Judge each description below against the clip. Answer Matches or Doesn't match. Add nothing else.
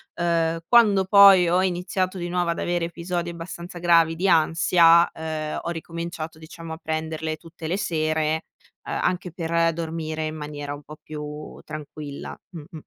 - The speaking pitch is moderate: Matches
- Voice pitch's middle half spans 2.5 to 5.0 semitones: Doesn't match